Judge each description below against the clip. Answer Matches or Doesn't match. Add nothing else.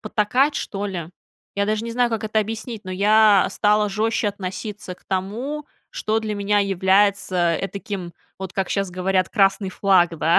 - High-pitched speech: Matches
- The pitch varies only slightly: Matches